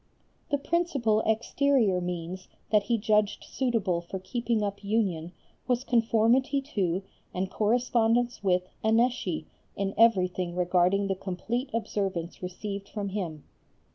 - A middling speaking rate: No, slow, 120 wpm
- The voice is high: Yes, high, 205 Hz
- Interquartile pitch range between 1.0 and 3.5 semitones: No, average, 4.3 semitones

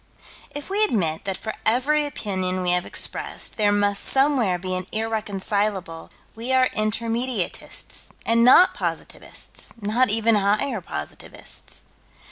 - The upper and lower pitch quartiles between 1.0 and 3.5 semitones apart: No, average, 4.5 semitones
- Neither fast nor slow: No, slow, 125 wpm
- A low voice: No, high, 215 Hz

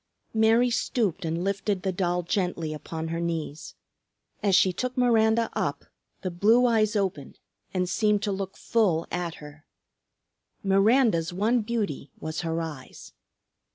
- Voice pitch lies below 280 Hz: Yes, high, 190 Hz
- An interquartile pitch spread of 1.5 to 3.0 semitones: No, average, 4.8 semitones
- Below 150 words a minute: Yes, average, 140 wpm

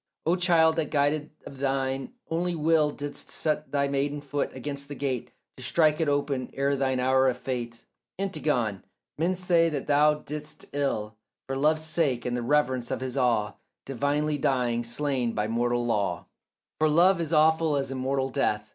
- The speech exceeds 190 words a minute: No, average, 175 wpm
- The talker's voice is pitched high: No, medium, 140 Hz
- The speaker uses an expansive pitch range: No, average, 3.2 semitones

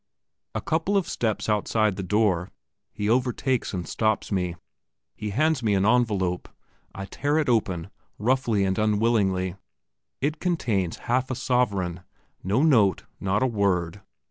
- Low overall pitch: Yes, low, 105 Hz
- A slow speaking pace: No, average, 145 wpm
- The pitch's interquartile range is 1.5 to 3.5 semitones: No, average, 4.6 semitones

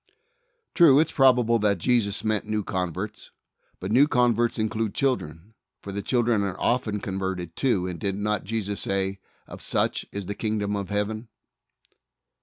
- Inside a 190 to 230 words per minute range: No, average, 165 wpm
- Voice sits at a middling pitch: No, low, 105 Hz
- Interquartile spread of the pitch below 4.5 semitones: Yes, average, 3.2 semitones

